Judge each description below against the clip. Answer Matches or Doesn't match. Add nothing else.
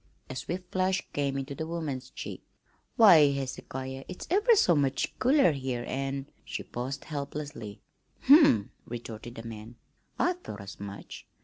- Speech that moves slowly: Doesn't match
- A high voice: Doesn't match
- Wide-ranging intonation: Matches